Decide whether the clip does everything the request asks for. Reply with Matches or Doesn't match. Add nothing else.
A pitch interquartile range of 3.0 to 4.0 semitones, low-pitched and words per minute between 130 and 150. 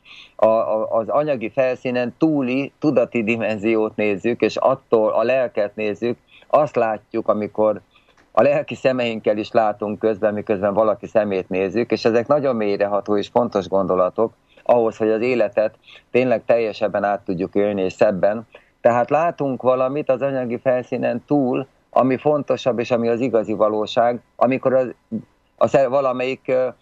Matches